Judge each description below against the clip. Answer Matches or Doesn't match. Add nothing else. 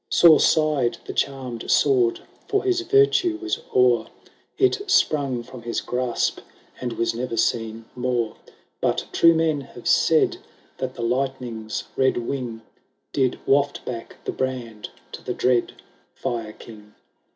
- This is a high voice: Doesn't match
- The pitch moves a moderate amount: Matches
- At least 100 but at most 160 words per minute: Matches